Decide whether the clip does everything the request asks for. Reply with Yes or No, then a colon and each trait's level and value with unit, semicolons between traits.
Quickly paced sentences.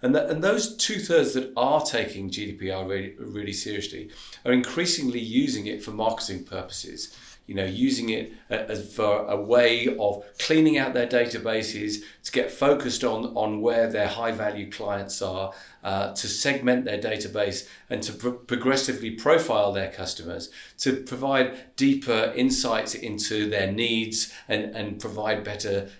No: average, 155 wpm